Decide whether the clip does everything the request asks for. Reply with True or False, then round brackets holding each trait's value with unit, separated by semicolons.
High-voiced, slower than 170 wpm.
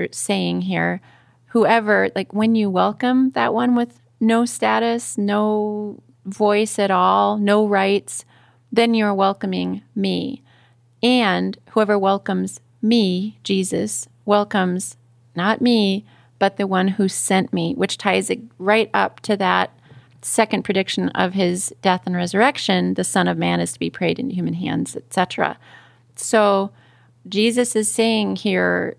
True (195 Hz; 140 wpm)